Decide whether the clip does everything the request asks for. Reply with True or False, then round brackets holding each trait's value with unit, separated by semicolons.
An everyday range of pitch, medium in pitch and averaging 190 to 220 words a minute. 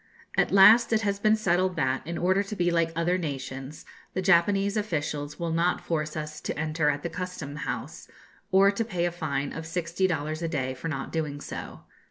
True (3.6 semitones; 170 Hz; 205 wpm)